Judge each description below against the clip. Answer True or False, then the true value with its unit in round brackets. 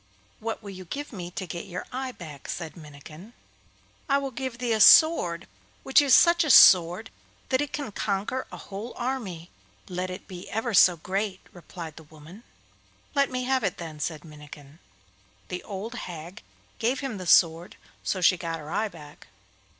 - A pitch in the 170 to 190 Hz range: True (185 Hz)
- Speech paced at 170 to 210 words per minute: True (180 wpm)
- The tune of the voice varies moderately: False (6.5 semitones)